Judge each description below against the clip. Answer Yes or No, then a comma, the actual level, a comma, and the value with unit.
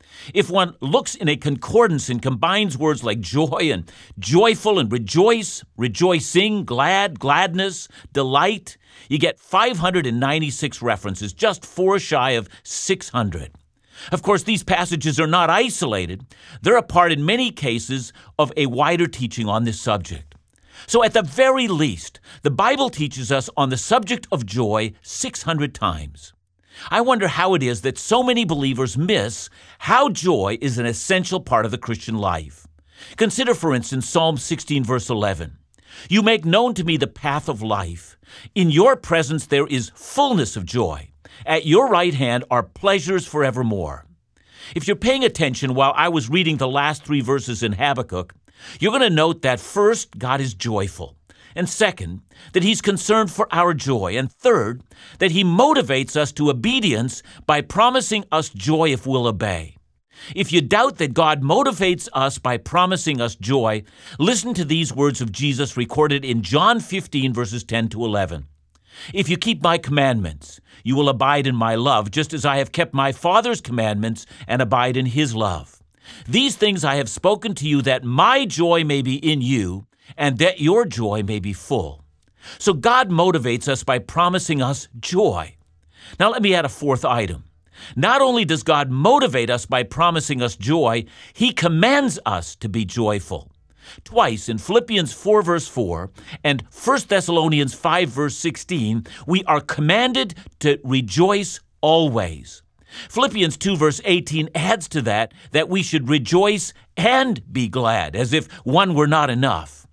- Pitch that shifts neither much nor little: No, wide, 7.5 semitones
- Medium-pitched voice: Yes, medium, 145 Hz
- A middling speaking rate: Yes, average, 165 wpm